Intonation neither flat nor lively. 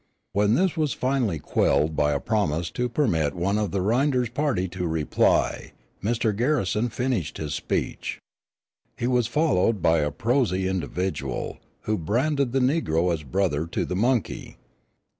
No: wide, 7.0 semitones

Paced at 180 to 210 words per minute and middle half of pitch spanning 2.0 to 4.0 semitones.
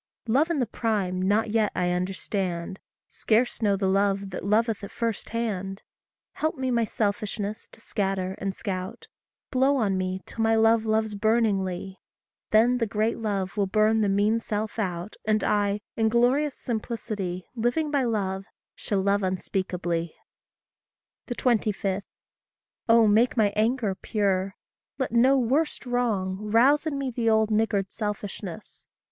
No: average, 145 wpm; average, 3.0 semitones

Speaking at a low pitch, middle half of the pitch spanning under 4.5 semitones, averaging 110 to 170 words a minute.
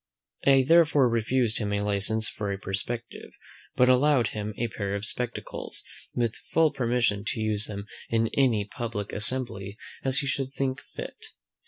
Yes: low, 115 Hz; average, 4.1 semitones; average, 160 wpm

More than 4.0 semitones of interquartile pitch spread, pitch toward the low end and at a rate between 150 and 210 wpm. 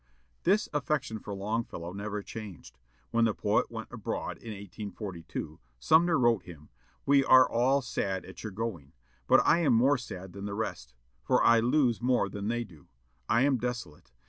Yes: average, 4.5 semitones; low, 110 Hz; average, 170 wpm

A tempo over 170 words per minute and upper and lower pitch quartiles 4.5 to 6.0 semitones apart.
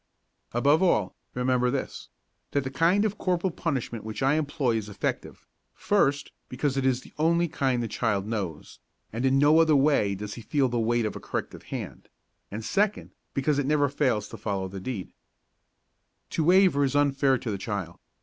Yes: average, 185 wpm; average, 5.1 semitones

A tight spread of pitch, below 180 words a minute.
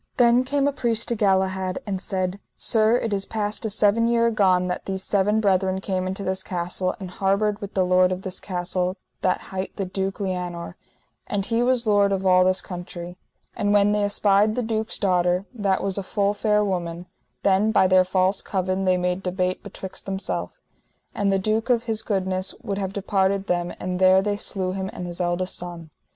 No: narrow, 2.0 semitones; average, 200 wpm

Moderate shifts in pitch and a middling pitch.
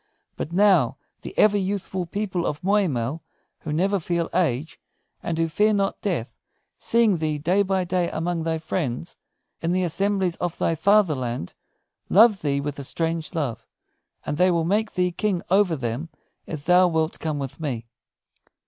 Yes: average, 4.0 semitones; medium, 170 Hz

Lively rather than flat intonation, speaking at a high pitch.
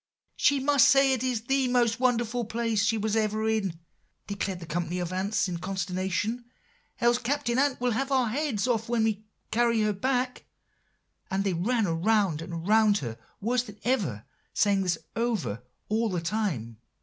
No: average, 4.4 semitones; high, 220 Hz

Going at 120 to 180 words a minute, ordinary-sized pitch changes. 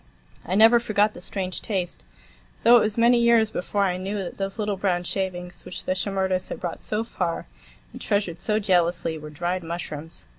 No: average, 190 wpm; average, 3.0 semitones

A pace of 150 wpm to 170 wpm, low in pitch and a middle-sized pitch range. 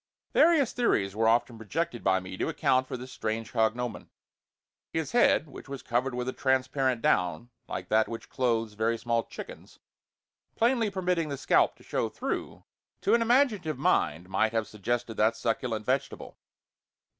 Yes: average, 160 wpm; low, 120 Hz; average, 4.4 semitones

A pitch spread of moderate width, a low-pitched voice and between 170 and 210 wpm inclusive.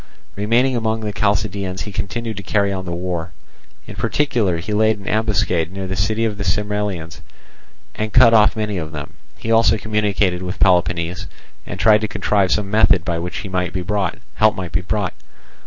Yes: average, 3.0 semitones; low, 100 Hz; average, 175 wpm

